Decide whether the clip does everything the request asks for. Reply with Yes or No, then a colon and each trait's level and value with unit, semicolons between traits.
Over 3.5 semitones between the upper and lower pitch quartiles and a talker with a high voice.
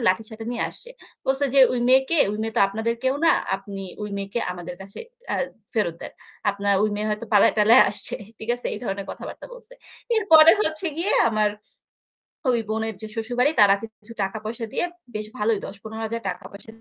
No: average, 3.2 semitones; high, 220 Hz